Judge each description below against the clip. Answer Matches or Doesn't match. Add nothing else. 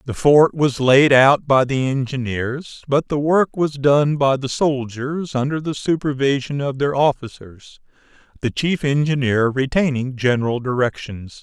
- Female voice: Doesn't match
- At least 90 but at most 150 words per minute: Matches